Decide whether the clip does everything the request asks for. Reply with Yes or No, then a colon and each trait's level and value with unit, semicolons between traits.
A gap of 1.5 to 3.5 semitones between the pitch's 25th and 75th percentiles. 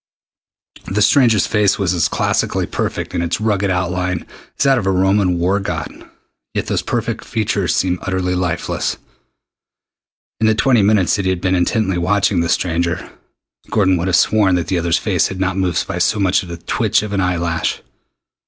Yes: narrow, 2.6 semitones